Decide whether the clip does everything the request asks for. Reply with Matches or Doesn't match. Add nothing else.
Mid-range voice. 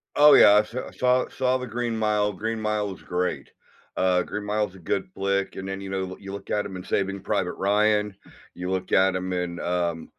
Doesn't match